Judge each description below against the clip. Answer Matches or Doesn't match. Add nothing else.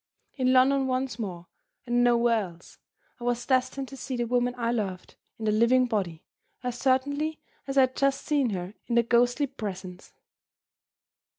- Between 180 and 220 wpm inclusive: Doesn't match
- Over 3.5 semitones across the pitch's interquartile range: Doesn't match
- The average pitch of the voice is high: Matches